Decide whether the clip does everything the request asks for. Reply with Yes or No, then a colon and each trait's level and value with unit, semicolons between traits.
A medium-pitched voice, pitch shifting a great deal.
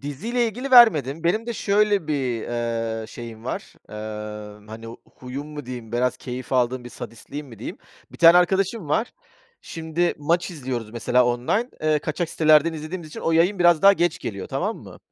Yes: medium, 145 Hz; wide, 6.5 semitones